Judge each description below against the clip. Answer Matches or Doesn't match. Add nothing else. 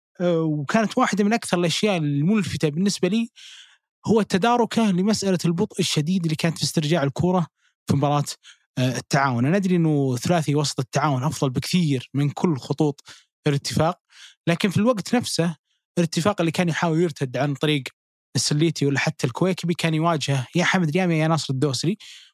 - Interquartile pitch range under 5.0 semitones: Matches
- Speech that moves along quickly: Matches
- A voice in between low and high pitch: Matches